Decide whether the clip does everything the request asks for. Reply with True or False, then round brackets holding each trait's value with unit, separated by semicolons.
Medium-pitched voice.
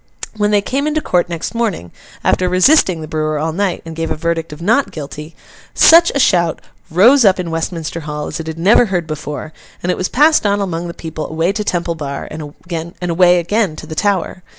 True (170 Hz)